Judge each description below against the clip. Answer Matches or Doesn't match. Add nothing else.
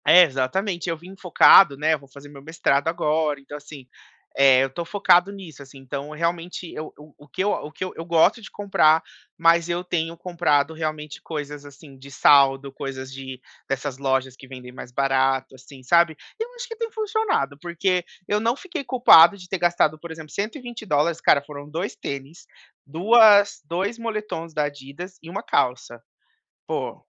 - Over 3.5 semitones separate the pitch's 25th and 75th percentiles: Matches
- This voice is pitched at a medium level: Matches